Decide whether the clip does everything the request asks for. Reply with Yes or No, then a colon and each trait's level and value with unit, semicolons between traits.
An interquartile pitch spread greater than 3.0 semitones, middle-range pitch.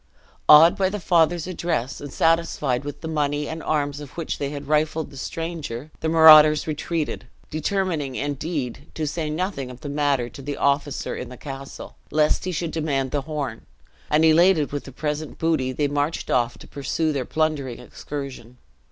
No: narrow, 2.4 semitones; medium, 150 Hz